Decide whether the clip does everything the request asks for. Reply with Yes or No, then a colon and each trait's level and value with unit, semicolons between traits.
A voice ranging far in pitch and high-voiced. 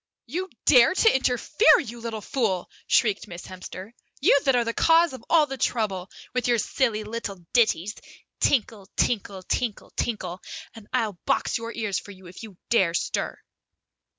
No: average, 4.5 semitones; high, 230 Hz